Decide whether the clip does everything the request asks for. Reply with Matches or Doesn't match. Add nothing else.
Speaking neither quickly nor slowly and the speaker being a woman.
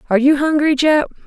Matches